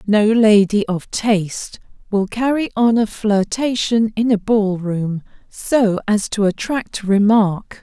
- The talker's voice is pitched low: No, high, 215 Hz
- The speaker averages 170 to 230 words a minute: No, average, 140 wpm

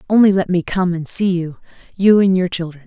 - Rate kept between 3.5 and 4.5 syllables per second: No, 5.5 syllables/s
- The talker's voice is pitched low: No, medium, 180 Hz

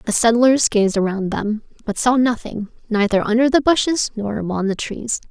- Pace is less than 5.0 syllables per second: Yes, 4.8 syllables/s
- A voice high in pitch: Yes, high, 225 Hz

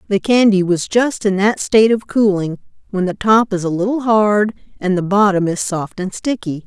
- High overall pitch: Yes, high, 200 Hz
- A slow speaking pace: No, fast, 205 wpm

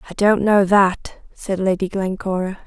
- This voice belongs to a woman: Yes, female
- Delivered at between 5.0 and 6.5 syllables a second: No, 4.4 syllables/s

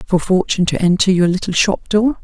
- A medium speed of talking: No, fast, 215 wpm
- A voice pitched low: No, high, 190 Hz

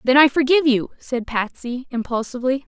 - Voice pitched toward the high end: Yes, very high, 260 Hz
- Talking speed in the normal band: Yes, average, 155 wpm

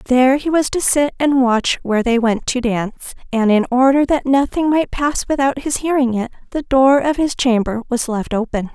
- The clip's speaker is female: Yes, female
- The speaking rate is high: Yes, fast, 215 wpm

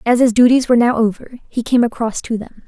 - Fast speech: Yes, fast, 245 wpm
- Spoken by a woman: Yes, female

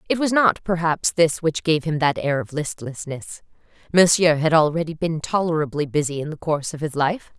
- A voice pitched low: No, medium, 160 Hz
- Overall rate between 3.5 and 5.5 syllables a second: Yes, 5.3 syllables/s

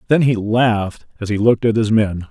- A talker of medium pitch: No, low, 110 Hz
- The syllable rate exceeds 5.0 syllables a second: Yes, 5.6 syllables/s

